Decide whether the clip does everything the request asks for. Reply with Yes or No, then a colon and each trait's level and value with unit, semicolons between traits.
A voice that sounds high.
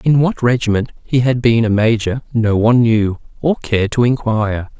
No: low, 115 Hz